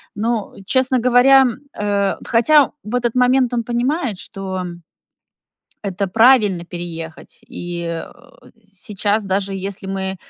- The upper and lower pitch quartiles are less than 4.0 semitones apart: No, average, 4.4 semitones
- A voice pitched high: Yes, high, 210 Hz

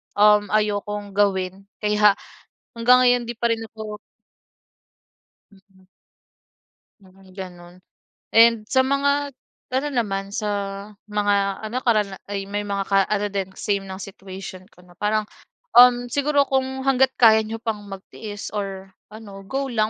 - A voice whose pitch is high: Yes, high, 210 Hz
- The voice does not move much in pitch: No, average, 3.4 semitones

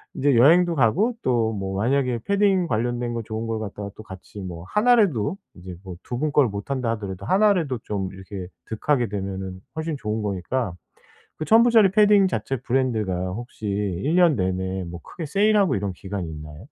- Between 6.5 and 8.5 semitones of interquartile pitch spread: Yes, wide, 8.2 semitones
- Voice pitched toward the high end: No, low, 115 Hz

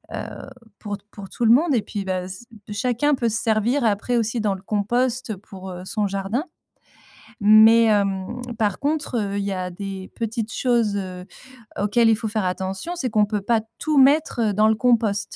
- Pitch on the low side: No, high, 215 Hz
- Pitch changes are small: No, average, 3.2 semitones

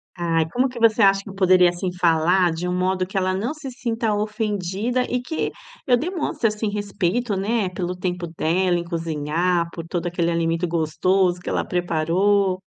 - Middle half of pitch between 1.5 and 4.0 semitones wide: Yes, average, 3.4 semitones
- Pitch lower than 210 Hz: Yes, medium, 185 Hz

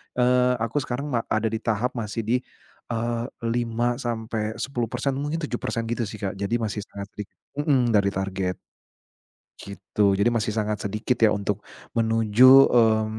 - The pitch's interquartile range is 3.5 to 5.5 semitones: No, narrow, 2.5 semitones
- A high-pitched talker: No, low, 115 Hz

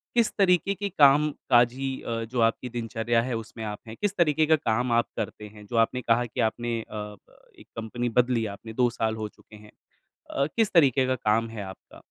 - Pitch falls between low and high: No, low, 120 Hz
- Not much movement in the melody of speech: No, average, 3.5 semitones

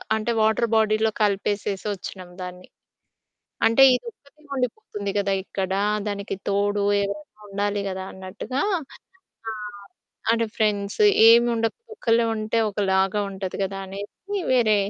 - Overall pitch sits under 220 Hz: Yes, high, 205 Hz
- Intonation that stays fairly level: Yes, narrow, 2.2 semitones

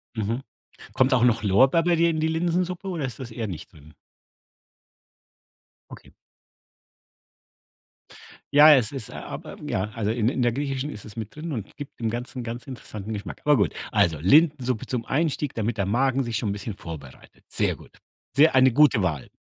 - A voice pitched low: Yes, low, 120 Hz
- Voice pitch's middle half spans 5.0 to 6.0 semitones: Yes, average, 5.3 semitones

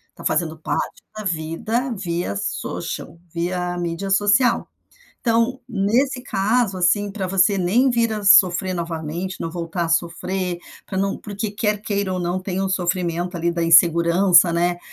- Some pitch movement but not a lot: Yes, average, 3.0 semitones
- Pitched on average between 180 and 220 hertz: Yes, medium, 185 Hz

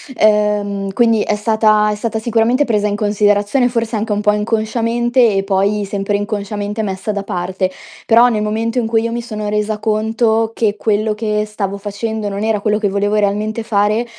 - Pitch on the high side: Yes, high, 210 Hz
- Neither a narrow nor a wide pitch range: No, narrow, 1.5 semitones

